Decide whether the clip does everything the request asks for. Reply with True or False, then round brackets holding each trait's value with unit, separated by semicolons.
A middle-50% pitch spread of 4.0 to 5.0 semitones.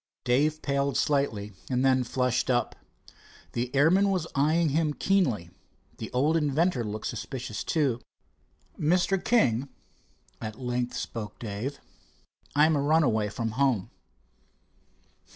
True (4.4 semitones)